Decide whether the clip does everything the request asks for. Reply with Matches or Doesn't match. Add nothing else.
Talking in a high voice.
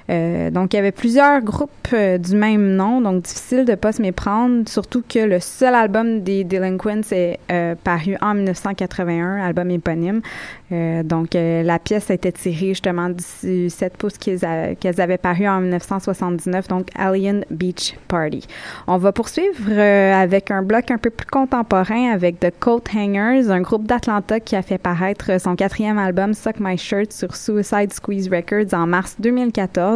Matches